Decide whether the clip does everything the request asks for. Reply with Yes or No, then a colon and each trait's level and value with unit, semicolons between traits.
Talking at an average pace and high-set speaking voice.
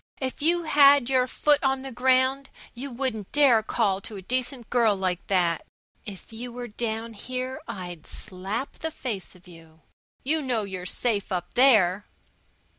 Yes: average, 165 wpm; high, 235 Hz